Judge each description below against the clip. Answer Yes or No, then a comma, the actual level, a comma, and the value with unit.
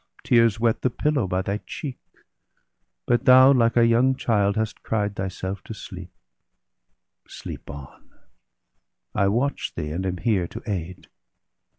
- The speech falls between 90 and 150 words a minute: Yes, average, 145 wpm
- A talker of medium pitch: No, low, 105 Hz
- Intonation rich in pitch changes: No, average, 4.2 semitones